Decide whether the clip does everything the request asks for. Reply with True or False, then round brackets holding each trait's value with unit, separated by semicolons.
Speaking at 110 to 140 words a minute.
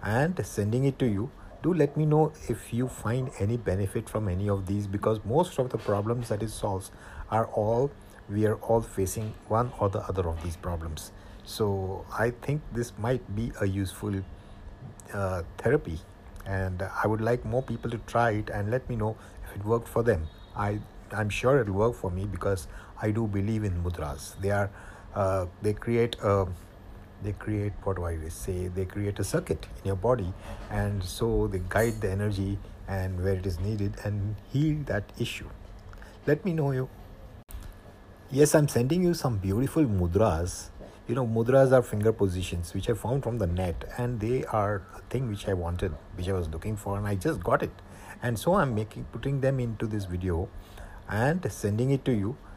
False (195 wpm)